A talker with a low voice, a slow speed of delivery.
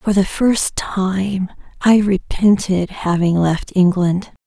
No: high, 190 Hz; slow, 120 wpm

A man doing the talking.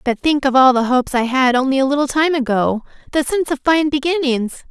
No: female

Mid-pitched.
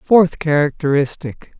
Yes: medium, 155 Hz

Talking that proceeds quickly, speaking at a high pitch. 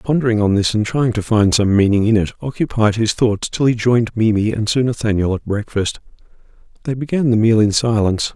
No: fast, 210 wpm; low, 110 Hz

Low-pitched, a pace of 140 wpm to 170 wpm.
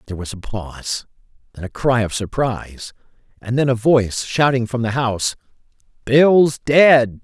Yes: low, 120 Hz; average, 160 wpm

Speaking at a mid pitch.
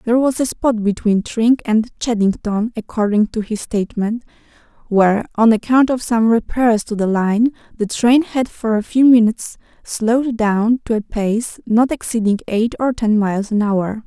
No: high, 225 Hz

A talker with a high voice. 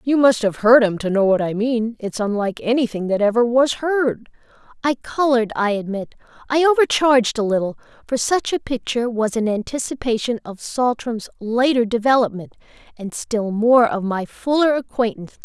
Yes: high, 235 Hz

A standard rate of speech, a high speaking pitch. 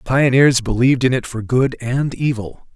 No: average, 195 wpm; low, 125 Hz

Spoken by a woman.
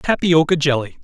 No: male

